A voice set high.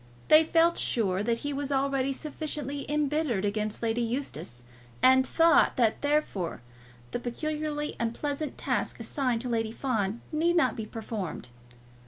Yes: very high, 260 Hz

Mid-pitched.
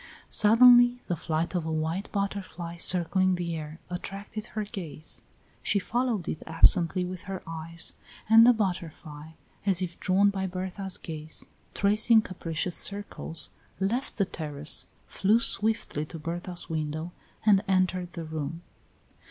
Yes: medium, 180 Hz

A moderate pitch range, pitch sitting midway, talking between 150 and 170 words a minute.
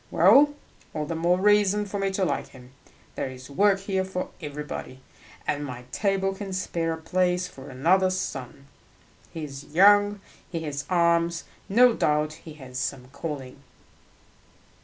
Yes: average, 5.0 semitones; medium, 170 Hz; average, 155 wpm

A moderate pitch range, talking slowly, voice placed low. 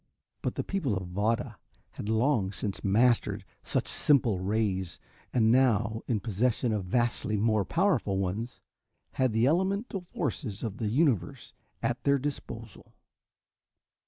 Yes: average, 4.0 semitones; slow, 130 wpm; low, 115 Hz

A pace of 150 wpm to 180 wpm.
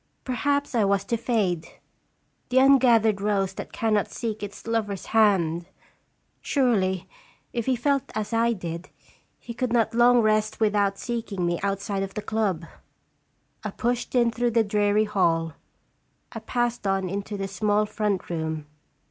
Yes: average, 155 wpm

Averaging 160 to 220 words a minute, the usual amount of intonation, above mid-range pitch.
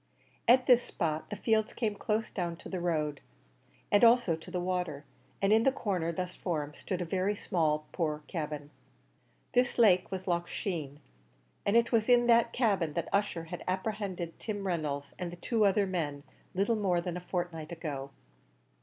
No: average, 180 wpm; average, 4.3 semitones; medium, 180 Hz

